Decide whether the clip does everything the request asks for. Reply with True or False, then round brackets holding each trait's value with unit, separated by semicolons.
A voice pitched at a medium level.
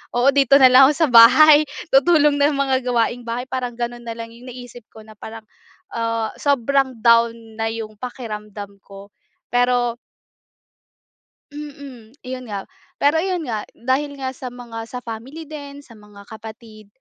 False (245 Hz)